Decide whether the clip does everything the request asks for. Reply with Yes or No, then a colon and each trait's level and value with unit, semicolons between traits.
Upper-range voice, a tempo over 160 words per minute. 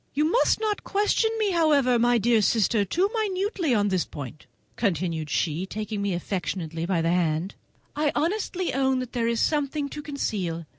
Yes: high, 235 Hz; average, 170 wpm